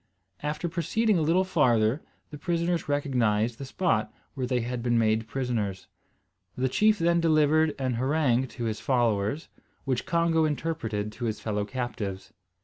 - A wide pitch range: Yes, wide, 5.9 semitones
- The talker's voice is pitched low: Yes, low, 130 Hz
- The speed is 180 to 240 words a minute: No, average, 150 wpm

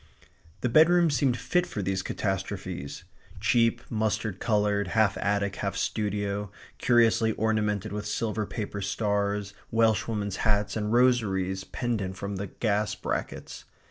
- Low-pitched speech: Yes, low, 105 Hz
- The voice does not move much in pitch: Yes, narrow, 2.2 semitones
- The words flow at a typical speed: No, slow, 125 wpm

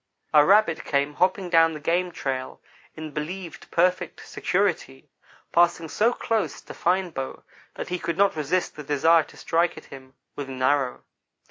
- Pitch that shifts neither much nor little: Yes, average, 3.9 semitones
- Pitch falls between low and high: Yes, medium, 165 Hz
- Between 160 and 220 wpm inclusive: Yes, average, 165 wpm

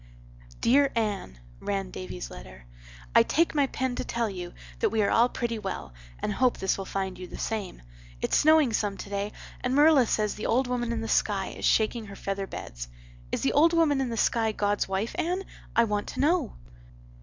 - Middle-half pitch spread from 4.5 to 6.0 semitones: Yes, average, 4.8 semitones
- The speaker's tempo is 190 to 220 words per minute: Yes, average, 200 wpm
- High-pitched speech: Yes, high, 220 Hz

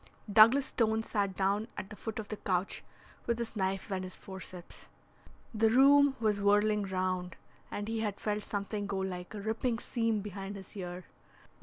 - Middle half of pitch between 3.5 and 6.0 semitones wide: No, narrow, 2.5 semitones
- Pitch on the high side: Yes, high, 205 Hz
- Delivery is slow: No, average, 175 wpm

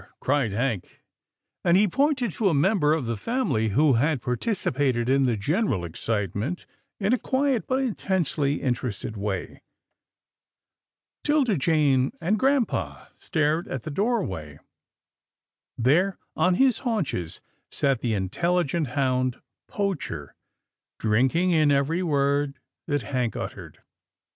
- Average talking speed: No, slow, 125 wpm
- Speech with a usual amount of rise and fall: No, wide, 7.6 semitones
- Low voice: No, medium, 145 Hz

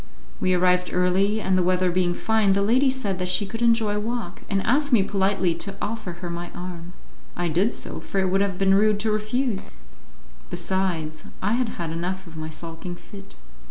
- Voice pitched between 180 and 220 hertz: Yes, high, 190 Hz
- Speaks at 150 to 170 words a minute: No, average, 200 wpm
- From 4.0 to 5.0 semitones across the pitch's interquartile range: No, average, 3.0 semitones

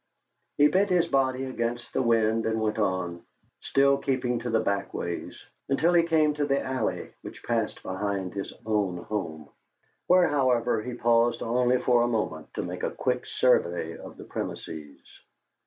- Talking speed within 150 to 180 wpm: Yes, average, 170 wpm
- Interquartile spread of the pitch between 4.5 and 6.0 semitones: Yes, average, 4.8 semitones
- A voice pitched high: No, low, 120 Hz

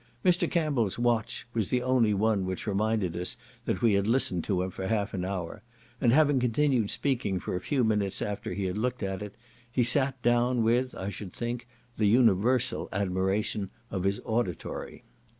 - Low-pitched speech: Yes, low, 110 Hz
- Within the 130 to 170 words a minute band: No, average, 185 wpm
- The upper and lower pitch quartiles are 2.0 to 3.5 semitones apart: No, average, 4.0 semitones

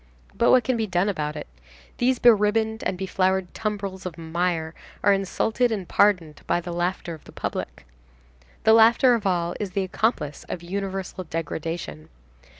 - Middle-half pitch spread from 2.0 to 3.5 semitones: No, average, 3.9 semitones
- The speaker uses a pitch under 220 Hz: Yes, high, 190 Hz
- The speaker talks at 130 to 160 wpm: No, average, 170 wpm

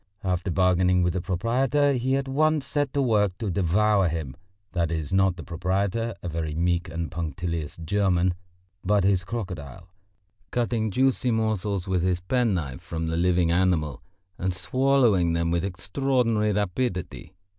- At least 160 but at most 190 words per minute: No, average, 150 wpm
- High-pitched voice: No, very low, 95 Hz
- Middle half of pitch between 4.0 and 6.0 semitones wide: Yes, average, 4.7 semitones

